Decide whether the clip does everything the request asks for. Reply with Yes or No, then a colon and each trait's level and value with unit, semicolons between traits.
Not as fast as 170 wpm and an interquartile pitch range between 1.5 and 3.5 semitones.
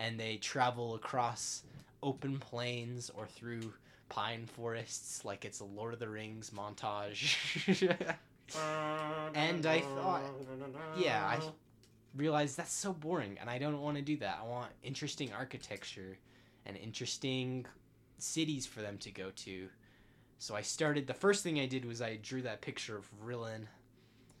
No: average, 150 wpm; average, 4.5 semitones